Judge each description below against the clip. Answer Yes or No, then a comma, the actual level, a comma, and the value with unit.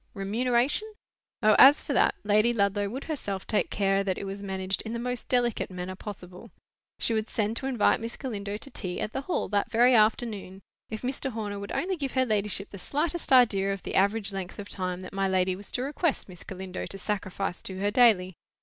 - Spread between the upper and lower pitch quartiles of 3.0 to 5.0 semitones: Yes, average, 3.8 semitones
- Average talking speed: No, fast, 215 wpm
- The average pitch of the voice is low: No, high, 205 Hz